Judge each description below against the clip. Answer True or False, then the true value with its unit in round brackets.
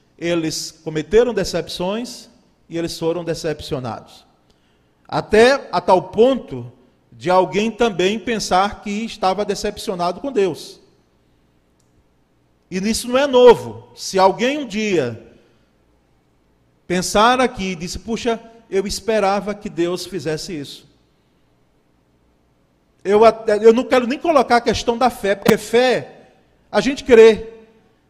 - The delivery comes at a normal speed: False (115 wpm)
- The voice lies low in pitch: False (190 Hz)